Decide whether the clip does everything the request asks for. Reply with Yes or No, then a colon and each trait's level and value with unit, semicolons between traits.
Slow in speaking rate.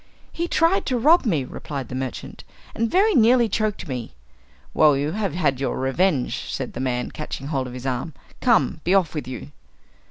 No: average, 190 wpm